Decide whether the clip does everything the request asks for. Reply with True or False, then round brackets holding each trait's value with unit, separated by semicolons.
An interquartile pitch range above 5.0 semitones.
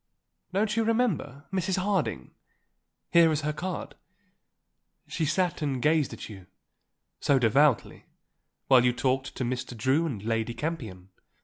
True (5.6 semitones)